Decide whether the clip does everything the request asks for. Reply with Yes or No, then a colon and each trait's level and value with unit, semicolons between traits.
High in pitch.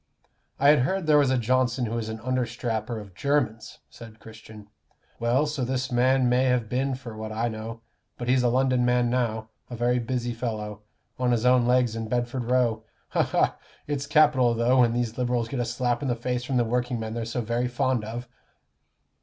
No: low, 120 Hz